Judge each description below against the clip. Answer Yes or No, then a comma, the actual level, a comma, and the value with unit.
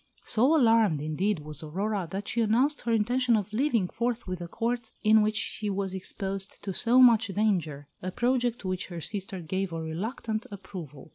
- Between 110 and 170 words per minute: No, average, 185 wpm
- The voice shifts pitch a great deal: No, average, 3.9 semitones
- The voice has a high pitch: Yes, high, 205 Hz